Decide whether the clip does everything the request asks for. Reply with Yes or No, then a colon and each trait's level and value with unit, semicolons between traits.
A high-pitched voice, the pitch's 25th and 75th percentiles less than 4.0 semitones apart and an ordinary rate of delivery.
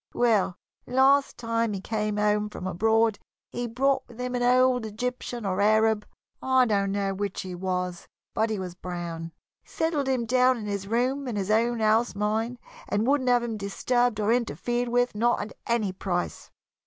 Yes: high, 225 Hz; average, 3.4 semitones; average, 180 wpm